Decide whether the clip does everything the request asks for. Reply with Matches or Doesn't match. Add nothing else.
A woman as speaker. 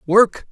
Doesn't match